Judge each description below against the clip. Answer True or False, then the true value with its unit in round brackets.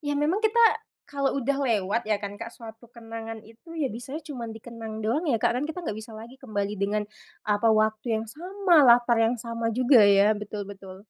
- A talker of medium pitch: False (230 Hz)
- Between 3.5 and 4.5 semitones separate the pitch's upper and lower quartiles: True (4.0 semitones)